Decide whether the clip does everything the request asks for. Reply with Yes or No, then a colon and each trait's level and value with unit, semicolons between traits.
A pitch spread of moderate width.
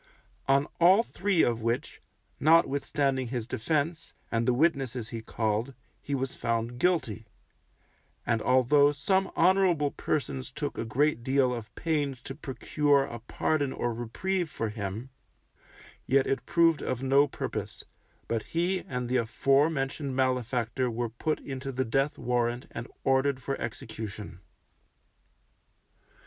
Yes: average, 3.8 semitones